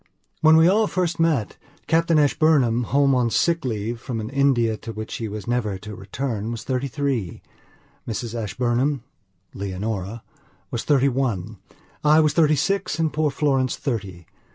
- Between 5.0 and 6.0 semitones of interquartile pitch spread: Yes, average, 5.3 semitones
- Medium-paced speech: Yes, average, 155 wpm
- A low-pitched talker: Yes, low, 125 Hz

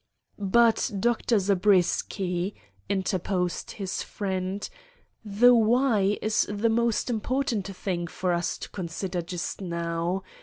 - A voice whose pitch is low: No, high, 195 Hz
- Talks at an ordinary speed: No, slow, 110 wpm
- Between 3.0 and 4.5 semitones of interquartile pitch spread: Yes, average, 3.5 semitones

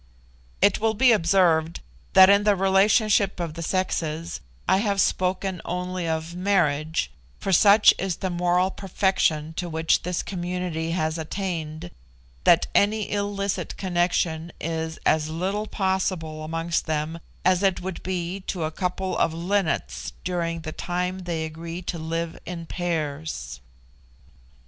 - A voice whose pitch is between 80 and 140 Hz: No, medium, 175 Hz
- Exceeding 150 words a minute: No, average, 140 wpm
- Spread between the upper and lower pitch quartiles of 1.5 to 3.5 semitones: Yes, average, 2.9 semitones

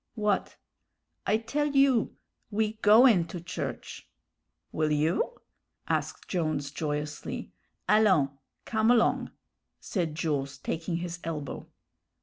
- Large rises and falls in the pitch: Yes, wide, 6.0 semitones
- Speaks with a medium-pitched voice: Yes, medium, 180 Hz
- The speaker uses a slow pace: Yes, slow, 105 wpm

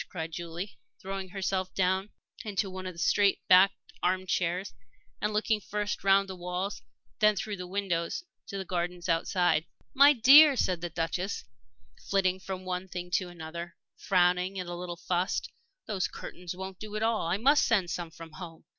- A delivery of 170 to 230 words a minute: Yes, average, 180 wpm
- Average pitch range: No, narrow, 2.0 semitones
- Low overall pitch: No, medium, 185 Hz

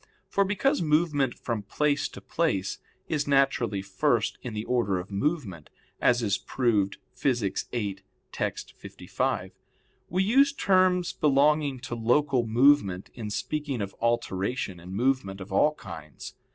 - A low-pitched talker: Yes, low, 125 Hz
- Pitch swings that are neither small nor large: No, wide, 7.0 semitones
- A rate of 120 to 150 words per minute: Yes, average, 140 wpm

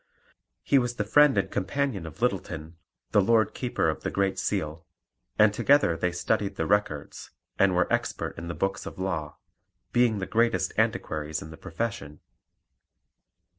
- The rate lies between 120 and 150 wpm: No, average, 160 wpm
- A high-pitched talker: No, very low, 95 Hz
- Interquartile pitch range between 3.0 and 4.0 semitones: No, average, 5.3 semitones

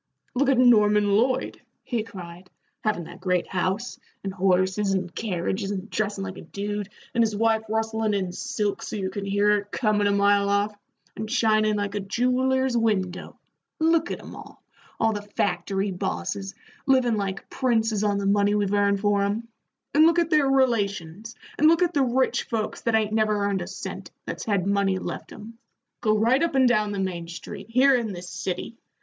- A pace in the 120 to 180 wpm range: No, average, 190 wpm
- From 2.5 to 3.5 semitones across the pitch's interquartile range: Yes, average, 2.8 semitones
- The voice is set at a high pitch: Yes, high, 210 Hz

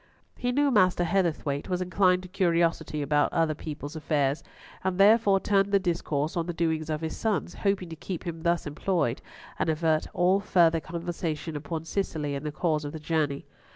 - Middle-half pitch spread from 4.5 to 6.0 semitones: No, average, 3.1 semitones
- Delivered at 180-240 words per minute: Yes, average, 185 wpm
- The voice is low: No, medium, 165 Hz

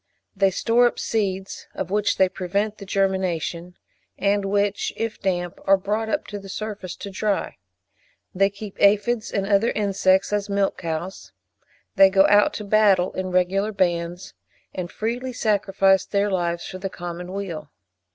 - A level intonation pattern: Yes, narrow, 1.8 semitones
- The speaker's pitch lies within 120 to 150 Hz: No, high, 195 Hz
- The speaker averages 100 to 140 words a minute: No, average, 160 wpm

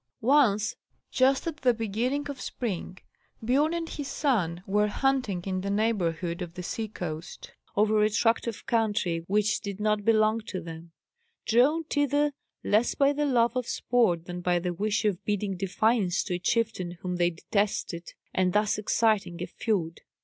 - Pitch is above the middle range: Yes, high, 210 Hz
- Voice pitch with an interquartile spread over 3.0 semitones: Yes, average, 5.1 semitones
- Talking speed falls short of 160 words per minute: No, average, 170 wpm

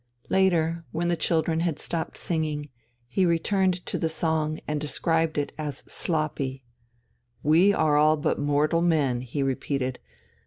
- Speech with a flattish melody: Yes, narrow, 2.3 semitones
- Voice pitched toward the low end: No, medium, 155 Hz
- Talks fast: No, average, 145 wpm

